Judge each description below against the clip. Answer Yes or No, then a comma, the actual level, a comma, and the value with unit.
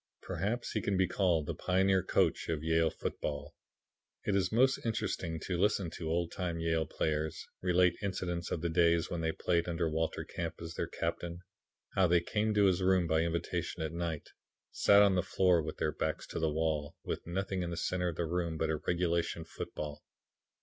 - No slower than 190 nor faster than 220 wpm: Yes, average, 200 wpm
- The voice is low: Yes, very low, 85 Hz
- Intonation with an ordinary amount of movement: No, narrow, 2.2 semitones